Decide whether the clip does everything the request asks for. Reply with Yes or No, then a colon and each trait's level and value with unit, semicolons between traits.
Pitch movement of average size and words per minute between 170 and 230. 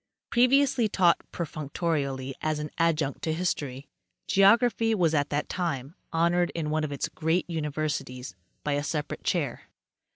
No: average, 3.5 semitones; average, 140 wpm